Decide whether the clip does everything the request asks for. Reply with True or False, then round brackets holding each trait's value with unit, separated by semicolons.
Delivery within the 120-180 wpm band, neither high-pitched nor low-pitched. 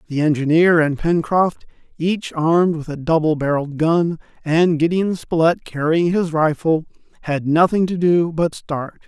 True (150 wpm; 160 Hz)